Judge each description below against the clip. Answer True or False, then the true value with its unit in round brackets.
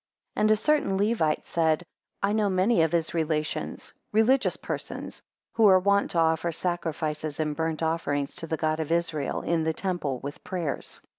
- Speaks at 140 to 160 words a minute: False (175 wpm)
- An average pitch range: True (3.7 semitones)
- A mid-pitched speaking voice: True (165 Hz)